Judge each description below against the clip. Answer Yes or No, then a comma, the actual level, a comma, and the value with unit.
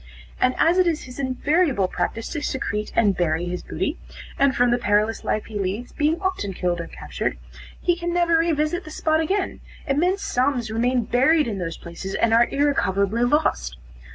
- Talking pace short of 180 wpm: No, average, 185 wpm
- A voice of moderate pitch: No, very high, 250 Hz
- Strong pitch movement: Yes, wide, 7.3 semitones